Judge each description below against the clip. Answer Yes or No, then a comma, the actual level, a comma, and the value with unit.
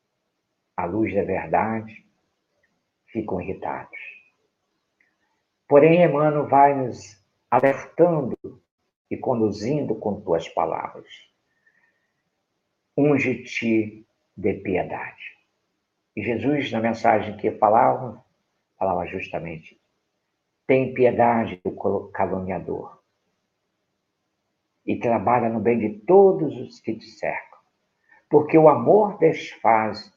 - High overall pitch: No, low, 120 Hz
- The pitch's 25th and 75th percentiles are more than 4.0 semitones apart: Yes, average, 5.2 semitones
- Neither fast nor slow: No, slow, 90 wpm